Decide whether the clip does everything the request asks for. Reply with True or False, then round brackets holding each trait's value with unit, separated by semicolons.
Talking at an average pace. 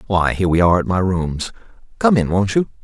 False (235 wpm)